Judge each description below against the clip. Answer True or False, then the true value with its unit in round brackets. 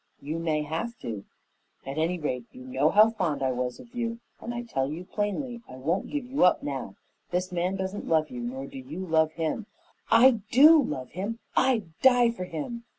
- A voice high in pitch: False (175 Hz)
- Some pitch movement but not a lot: False (8.3 semitones)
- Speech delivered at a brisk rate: True (210 wpm)